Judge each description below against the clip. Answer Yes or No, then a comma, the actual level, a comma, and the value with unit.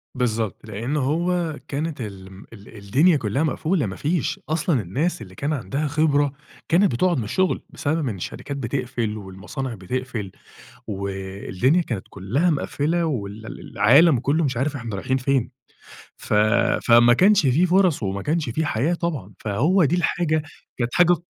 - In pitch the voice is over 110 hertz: Yes, low, 135 Hz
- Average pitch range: No, wide, 6.7 semitones